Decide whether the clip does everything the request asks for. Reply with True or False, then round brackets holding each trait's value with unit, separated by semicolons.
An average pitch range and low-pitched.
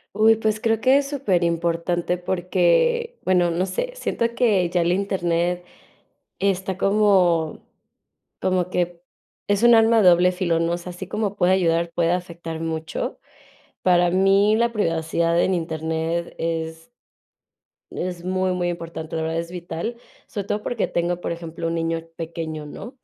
False (3.0 semitones; 175 Hz)